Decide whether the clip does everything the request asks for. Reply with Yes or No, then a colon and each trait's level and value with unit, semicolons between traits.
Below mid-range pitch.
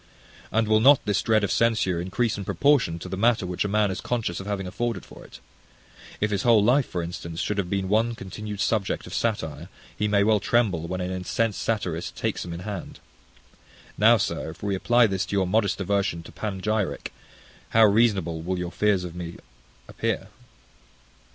Yes: low, 100 Hz